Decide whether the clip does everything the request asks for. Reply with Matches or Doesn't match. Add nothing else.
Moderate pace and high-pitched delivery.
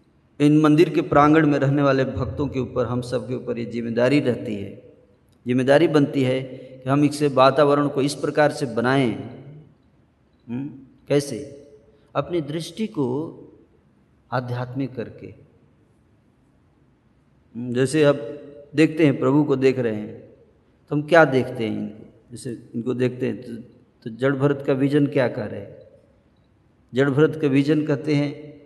Doesn't match